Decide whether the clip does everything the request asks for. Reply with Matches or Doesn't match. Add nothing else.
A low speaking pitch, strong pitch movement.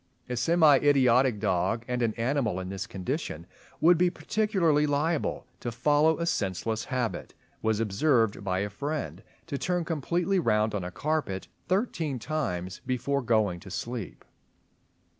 Matches